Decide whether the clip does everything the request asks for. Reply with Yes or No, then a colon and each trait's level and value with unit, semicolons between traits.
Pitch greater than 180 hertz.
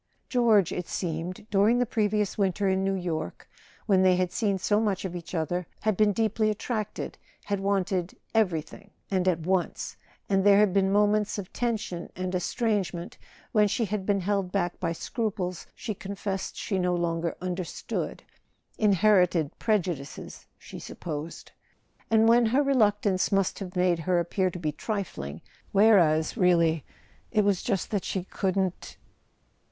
Yes: high, 190 Hz